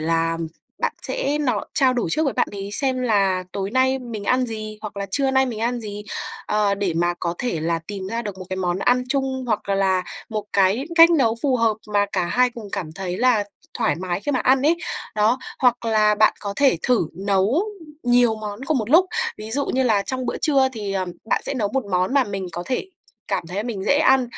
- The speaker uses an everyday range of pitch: Yes, average, 4.7 semitones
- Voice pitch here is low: No, high, 220 Hz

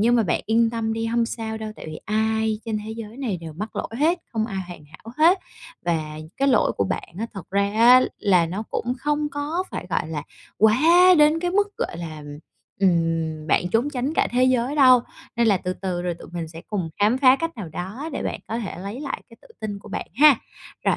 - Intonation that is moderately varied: No, wide, 6.1 semitones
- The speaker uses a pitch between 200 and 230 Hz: Yes, high, 220 Hz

